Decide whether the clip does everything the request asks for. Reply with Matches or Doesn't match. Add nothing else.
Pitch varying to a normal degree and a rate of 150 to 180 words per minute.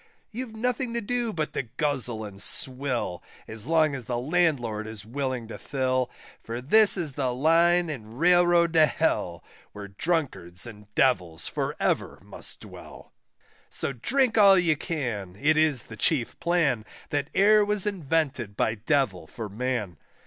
Doesn't match